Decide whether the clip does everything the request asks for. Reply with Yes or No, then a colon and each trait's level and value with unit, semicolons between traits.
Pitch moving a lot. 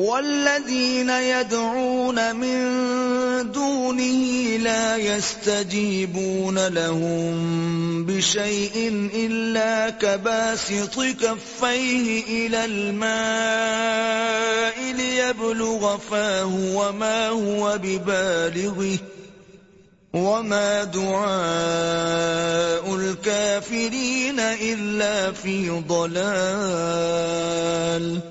No: average, 3.2 semitones